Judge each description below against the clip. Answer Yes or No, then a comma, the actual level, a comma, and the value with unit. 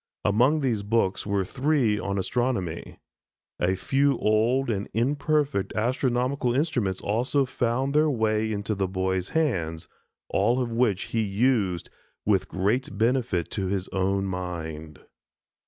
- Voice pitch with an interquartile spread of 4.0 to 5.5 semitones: Yes, average, 5.1 semitones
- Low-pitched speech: Yes, low, 110 Hz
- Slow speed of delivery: Yes, slow, 130 wpm